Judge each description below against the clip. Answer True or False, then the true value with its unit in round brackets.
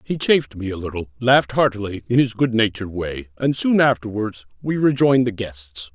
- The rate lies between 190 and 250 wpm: False (180 wpm)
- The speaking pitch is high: False (115 Hz)